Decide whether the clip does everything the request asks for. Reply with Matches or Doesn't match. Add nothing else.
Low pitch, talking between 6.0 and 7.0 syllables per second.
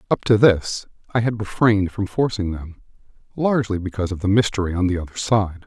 Matches